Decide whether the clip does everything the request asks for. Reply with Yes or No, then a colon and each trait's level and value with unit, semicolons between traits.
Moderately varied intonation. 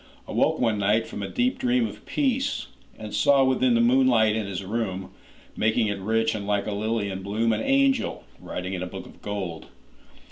Yes: average, 4.4 semitones